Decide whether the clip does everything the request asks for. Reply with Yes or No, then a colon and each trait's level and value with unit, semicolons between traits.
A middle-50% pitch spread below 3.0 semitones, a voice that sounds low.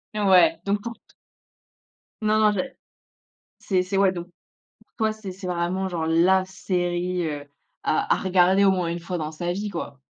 No: narrow, 2.4 semitones; medium, 185 Hz